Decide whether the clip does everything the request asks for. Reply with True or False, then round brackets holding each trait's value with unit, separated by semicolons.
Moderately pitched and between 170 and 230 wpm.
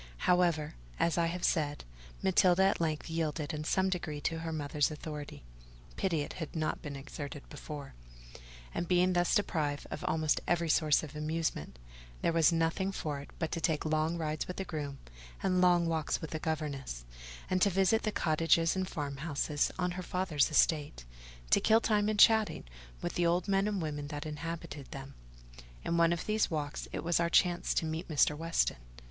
True (165 Hz; 185 wpm)